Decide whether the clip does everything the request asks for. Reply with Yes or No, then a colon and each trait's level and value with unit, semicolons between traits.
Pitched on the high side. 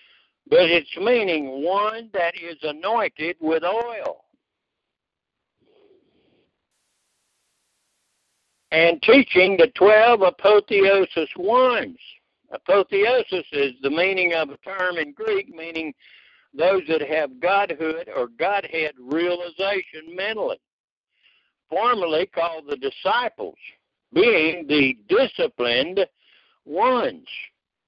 Yes: high, 195 Hz